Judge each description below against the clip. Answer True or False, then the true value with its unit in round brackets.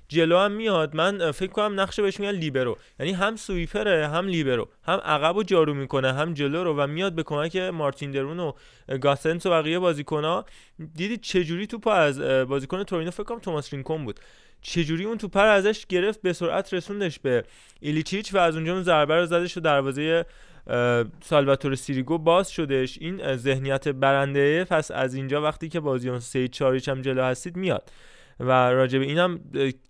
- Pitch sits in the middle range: True (160 Hz)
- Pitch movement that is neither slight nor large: True (4.9 semitones)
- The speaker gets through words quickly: True (175 wpm)